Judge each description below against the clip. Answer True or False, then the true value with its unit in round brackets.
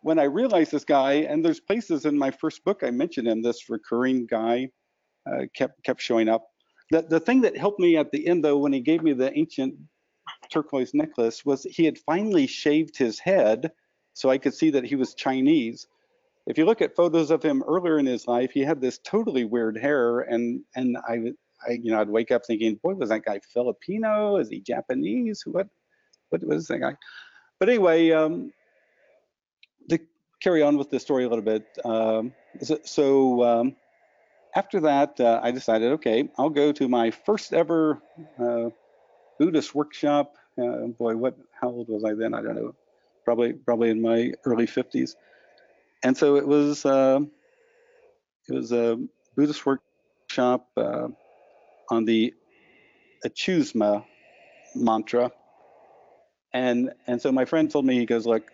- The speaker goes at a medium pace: True (170 wpm)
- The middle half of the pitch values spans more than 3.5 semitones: True (5.6 semitones)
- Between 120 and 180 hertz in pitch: True (140 Hz)